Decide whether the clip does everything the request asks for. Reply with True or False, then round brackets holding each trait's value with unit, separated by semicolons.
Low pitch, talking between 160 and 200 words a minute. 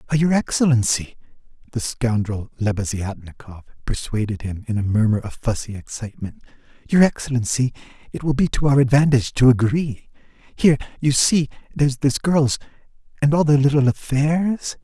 False (125 Hz; 135 wpm)